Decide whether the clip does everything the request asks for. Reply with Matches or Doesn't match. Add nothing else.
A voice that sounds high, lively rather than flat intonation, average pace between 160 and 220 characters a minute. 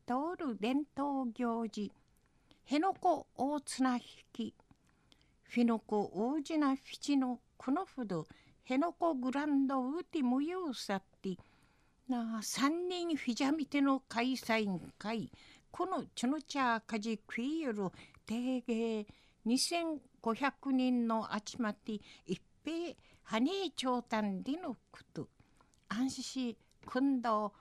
Doesn't match